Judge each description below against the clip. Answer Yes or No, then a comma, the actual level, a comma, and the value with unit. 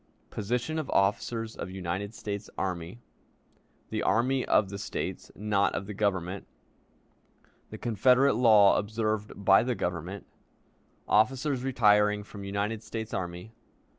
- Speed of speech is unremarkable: No, slow, 125 wpm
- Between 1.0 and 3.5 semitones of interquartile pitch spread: Yes, average, 2.9 semitones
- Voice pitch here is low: Yes, low, 105 Hz